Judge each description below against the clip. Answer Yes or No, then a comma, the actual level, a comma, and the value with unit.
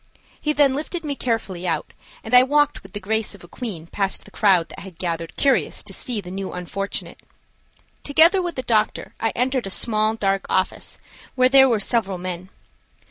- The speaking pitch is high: Yes, high, 215 Hz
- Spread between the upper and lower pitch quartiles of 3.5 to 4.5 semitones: No, wide, 5.6 semitones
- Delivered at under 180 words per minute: No, average, 190 wpm